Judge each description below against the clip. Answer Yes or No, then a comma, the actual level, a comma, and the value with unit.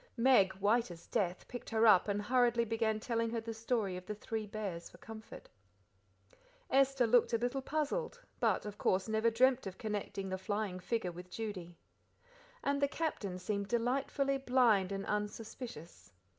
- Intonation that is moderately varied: Yes, average, 3.8 semitones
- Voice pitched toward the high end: Yes, high, 220 Hz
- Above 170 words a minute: No, average, 165 wpm